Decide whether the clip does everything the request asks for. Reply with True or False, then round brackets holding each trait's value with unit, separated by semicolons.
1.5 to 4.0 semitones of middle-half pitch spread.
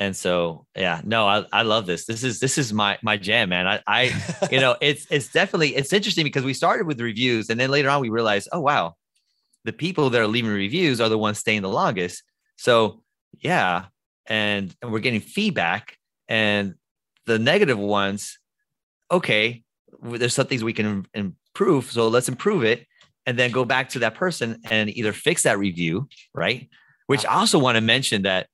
False (4.6 semitones)